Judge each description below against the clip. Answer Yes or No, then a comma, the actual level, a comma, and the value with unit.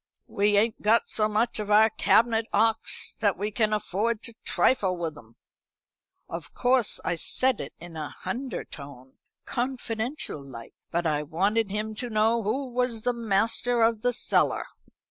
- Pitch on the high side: Yes, high, 215 Hz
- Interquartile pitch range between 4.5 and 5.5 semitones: No, average, 4.0 semitones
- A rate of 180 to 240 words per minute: No, average, 155 wpm